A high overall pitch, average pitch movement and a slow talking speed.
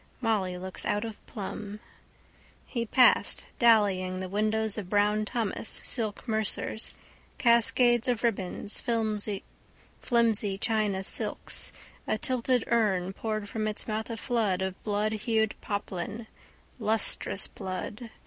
No: high, 215 Hz; narrow, 2.3 semitones; slow, 115 wpm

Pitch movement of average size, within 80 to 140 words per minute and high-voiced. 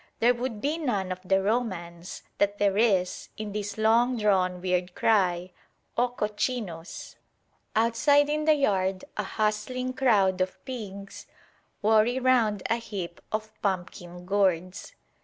Yes: average, 4.3 semitones; slow, 135 wpm; high, 210 Hz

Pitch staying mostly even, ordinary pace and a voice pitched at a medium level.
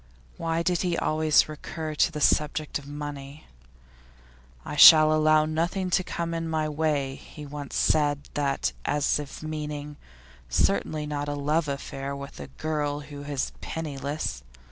Yes: narrow, 1.5 semitones; average, 150 wpm; medium, 150 Hz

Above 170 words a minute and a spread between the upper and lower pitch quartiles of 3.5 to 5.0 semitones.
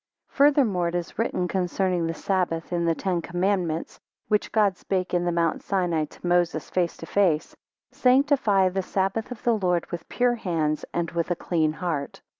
No: average, 180 wpm; average, 2.8 semitones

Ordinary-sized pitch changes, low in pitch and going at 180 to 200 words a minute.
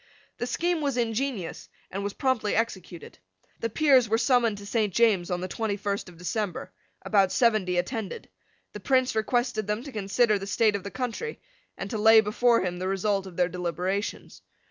No: average, 3.6 semitones; high, 210 Hz; average, 185 wpm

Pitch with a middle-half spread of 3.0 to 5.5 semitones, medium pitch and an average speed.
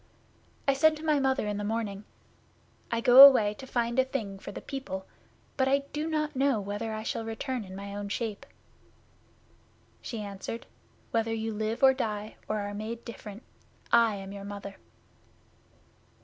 No: average, 4.4 semitones; high, 225 Hz; average, 170 wpm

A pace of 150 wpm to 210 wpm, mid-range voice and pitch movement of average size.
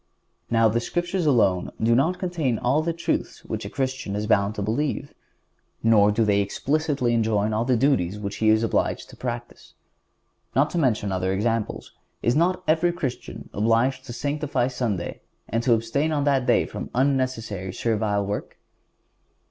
No: average, 165 wpm; low, 120 Hz; average, 4.8 semitones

